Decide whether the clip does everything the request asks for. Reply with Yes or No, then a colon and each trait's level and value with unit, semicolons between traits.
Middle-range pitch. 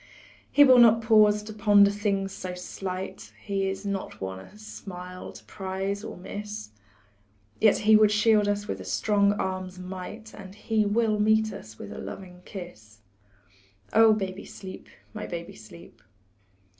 No: high, 200 Hz